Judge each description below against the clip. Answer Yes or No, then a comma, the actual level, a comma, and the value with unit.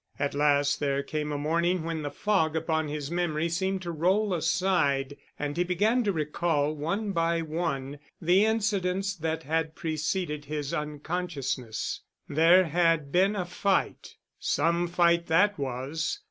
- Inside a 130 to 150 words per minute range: Yes, average, 145 wpm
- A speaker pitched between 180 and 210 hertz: No, medium, 165 Hz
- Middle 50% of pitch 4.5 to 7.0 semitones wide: No, average, 3.4 semitones